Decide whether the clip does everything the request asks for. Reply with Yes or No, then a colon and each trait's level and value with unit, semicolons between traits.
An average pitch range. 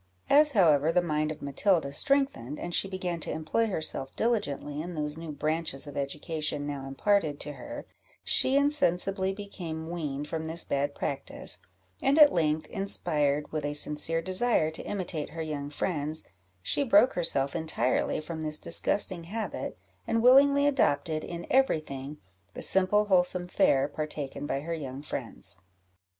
Yes: average, 4.7 semitones